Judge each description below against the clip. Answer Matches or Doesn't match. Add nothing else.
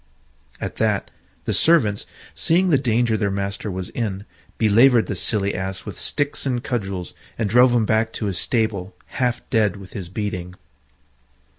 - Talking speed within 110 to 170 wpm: Matches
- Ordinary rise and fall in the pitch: Matches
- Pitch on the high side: Doesn't match